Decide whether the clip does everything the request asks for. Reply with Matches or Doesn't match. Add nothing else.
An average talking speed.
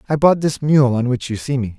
Doesn't match